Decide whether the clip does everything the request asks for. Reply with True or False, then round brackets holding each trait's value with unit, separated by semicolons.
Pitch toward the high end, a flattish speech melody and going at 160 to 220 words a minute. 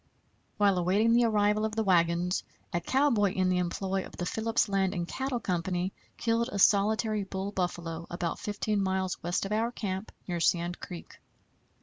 False (195 Hz; 3.3 semitones; 175 wpm)